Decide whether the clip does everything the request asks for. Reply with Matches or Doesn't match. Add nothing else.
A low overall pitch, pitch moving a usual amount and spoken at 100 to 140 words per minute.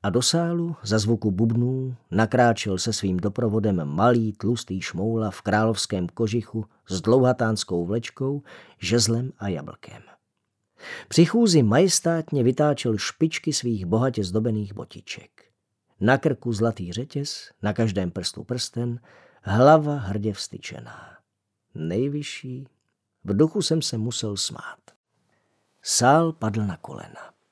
Matches